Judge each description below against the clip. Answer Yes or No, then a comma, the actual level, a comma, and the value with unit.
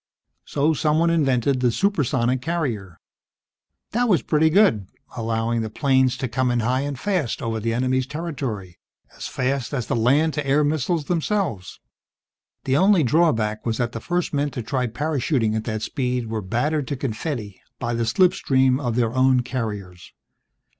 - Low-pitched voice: Yes, low, 130 Hz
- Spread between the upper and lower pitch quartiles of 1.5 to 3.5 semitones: No, average, 4.6 semitones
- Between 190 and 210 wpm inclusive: No, average, 165 wpm